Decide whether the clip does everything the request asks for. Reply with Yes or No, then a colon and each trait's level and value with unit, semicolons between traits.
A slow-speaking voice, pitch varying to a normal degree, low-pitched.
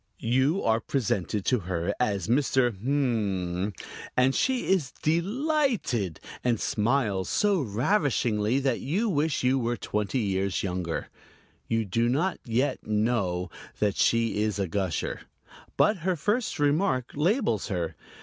No: slow, 130 wpm; wide, 6.3 semitones; low, 120 Hz